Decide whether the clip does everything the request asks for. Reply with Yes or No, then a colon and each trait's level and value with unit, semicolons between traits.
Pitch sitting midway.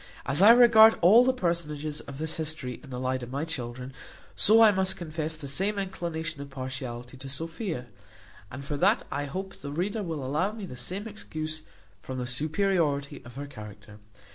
Yes: medium, 155 Hz